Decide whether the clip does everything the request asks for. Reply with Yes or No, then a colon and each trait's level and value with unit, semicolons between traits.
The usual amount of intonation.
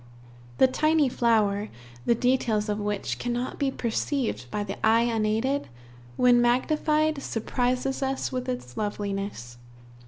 Yes: average, 3.9 semitones